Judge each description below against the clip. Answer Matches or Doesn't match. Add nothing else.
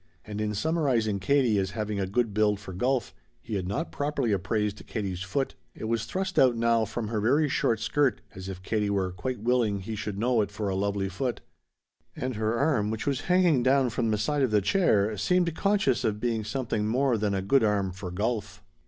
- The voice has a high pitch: Doesn't match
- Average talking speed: Doesn't match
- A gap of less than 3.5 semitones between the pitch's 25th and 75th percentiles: Doesn't match